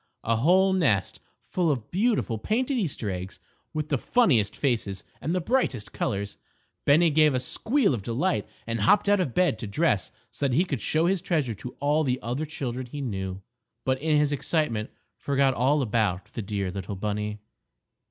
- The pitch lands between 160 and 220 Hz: No, low, 135 Hz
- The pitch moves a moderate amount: No, wide, 7.2 semitones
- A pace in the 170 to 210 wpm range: Yes, average, 180 wpm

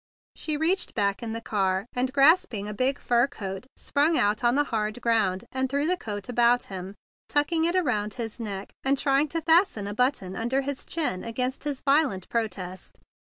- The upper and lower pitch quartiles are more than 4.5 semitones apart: Yes, wide, 5.5 semitones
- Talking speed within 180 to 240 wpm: Yes, average, 190 wpm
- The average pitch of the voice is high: Yes, high, 245 Hz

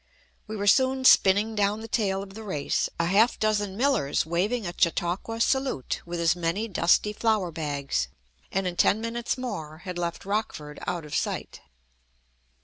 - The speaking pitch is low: No, high, 195 Hz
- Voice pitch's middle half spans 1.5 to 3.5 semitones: No, average, 4.6 semitones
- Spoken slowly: No, average, 165 wpm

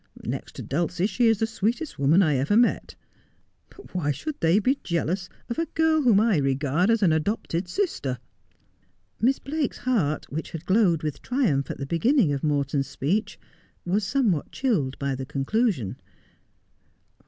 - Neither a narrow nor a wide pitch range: No, wide, 8.1 semitones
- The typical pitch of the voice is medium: Yes, medium, 180 Hz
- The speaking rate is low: No, average, 165 wpm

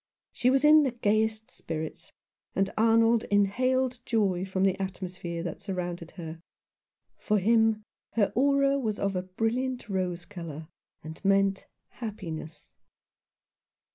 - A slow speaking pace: Yes, slow, 125 wpm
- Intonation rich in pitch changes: No, average, 4.1 semitones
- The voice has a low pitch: No, high, 200 Hz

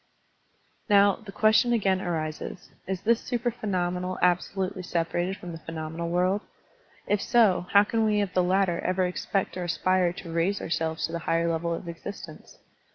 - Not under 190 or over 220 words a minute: No, average, 175 wpm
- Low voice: No, medium, 185 Hz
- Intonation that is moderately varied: Yes, average, 3.0 semitones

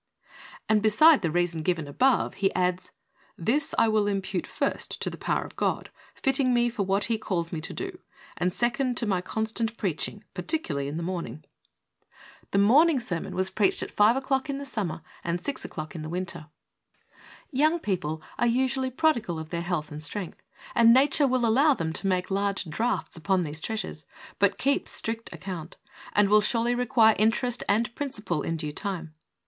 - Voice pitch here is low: No, high, 205 Hz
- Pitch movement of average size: No, wide, 5.8 semitones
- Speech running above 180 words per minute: Yes, average, 190 wpm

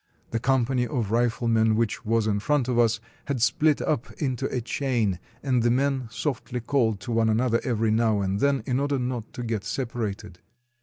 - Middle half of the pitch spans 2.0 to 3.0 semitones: Yes, average, 2.7 semitones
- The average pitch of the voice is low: Yes, low, 120 Hz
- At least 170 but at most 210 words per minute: Yes, average, 190 wpm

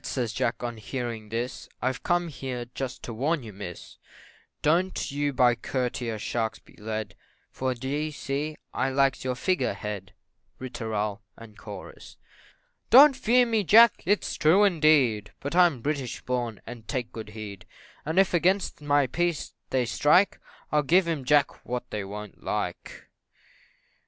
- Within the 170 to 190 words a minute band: No, average, 150 wpm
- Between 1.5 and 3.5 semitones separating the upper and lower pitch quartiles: No, wide, 5.4 semitones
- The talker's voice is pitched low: Yes, low, 130 Hz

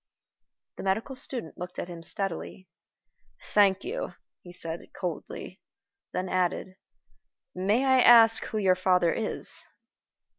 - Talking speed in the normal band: No, slow, 120 wpm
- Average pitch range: Yes, average, 3.8 semitones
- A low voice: No, high, 190 Hz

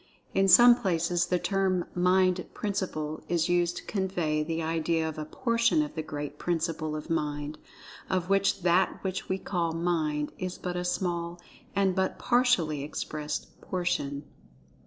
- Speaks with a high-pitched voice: No, medium, 175 Hz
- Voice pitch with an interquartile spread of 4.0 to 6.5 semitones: No, average, 3.2 semitones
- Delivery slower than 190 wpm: Yes, average, 155 wpm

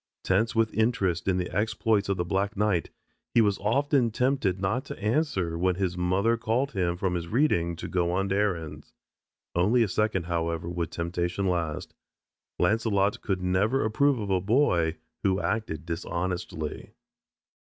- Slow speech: No, average, 155 wpm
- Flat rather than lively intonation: No, average, 4.1 semitones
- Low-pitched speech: Yes, very low, 95 Hz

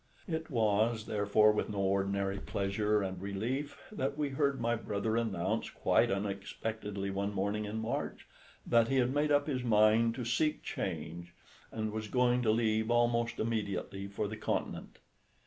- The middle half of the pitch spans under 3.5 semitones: Yes, average, 3.0 semitones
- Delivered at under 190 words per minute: Yes, average, 160 wpm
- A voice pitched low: Yes, low, 110 Hz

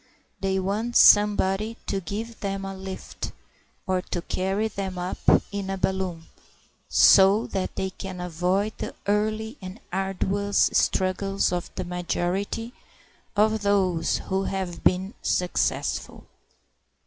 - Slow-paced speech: Yes, slow, 125 wpm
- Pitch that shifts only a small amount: Yes, narrow, 1.6 semitones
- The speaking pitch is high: Yes, high, 195 Hz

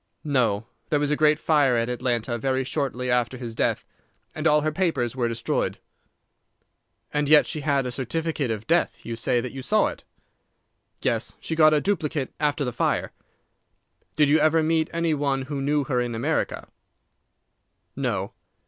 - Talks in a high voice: No, medium, 140 Hz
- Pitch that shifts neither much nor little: Yes, average, 3.9 semitones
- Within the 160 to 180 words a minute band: Yes, average, 170 wpm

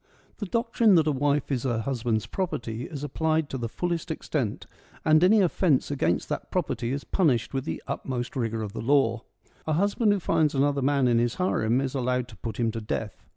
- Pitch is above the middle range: No, low, 135 Hz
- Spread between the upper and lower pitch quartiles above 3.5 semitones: Yes, average, 5.2 semitones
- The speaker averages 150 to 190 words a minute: No, fast, 205 wpm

